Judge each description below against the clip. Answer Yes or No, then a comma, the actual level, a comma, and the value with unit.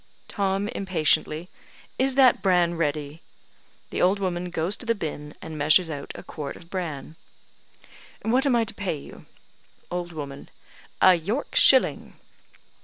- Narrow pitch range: No, average, 4.2 semitones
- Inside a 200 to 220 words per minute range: No, average, 145 wpm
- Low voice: No, medium, 175 Hz